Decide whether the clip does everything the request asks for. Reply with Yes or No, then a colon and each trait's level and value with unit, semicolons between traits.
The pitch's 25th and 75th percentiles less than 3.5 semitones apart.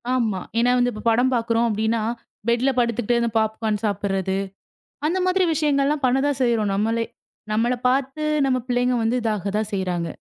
Yes: average, 3.1 semitones